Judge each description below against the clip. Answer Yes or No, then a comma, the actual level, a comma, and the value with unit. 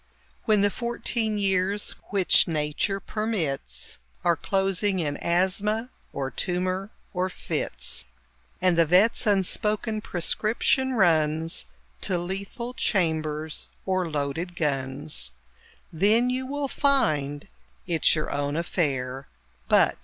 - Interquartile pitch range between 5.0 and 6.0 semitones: Yes, average, 5.3 semitones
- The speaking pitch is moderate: Yes, medium, 180 Hz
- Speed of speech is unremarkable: No, slow, 110 wpm